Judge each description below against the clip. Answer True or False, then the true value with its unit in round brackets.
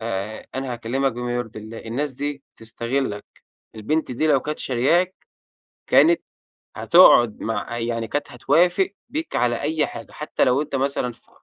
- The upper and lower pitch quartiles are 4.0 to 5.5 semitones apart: True (4.3 semitones)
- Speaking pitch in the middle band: False (125 Hz)